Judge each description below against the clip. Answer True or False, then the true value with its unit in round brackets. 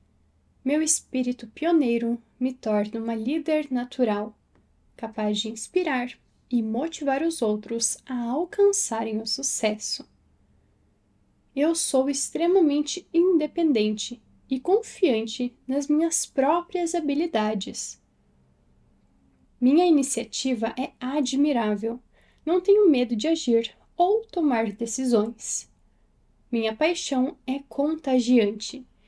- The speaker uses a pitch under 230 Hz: False (260 Hz)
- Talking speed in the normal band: False (95 wpm)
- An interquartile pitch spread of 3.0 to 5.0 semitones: False (5.5 semitones)